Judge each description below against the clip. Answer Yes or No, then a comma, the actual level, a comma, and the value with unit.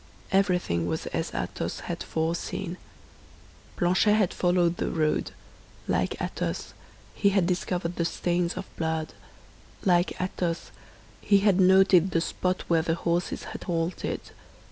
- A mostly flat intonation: Yes, narrow, 1.9 semitones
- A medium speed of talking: No, slow, 130 wpm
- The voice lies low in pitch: No, medium, 175 Hz